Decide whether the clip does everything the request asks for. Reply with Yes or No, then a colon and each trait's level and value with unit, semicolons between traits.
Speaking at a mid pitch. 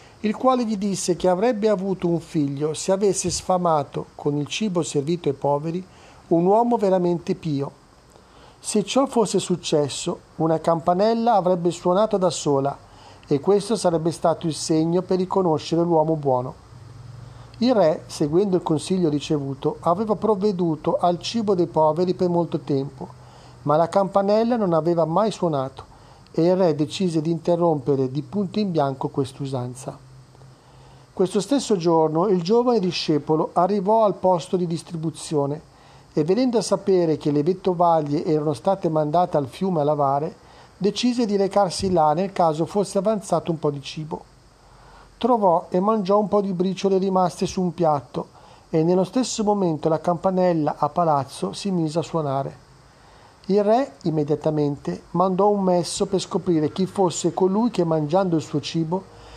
Yes: medium, 175 Hz